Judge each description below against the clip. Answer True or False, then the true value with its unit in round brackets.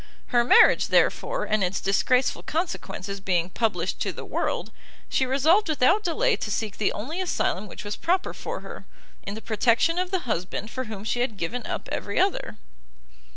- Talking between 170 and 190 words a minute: True (180 wpm)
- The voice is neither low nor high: False (240 Hz)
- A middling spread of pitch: False (8.7 semitones)